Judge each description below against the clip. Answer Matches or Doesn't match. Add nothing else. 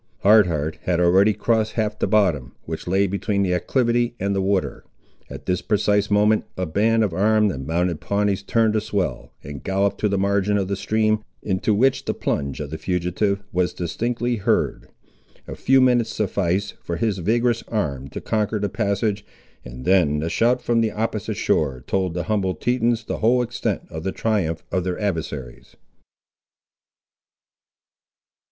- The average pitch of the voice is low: Matches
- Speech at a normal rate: Matches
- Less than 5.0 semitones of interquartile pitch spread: Matches